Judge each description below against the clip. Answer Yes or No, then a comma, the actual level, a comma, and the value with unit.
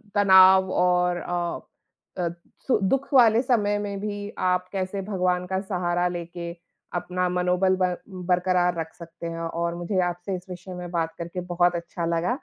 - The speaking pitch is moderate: Yes, medium, 180 Hz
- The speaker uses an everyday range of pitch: No, narrow, 1.5 semitones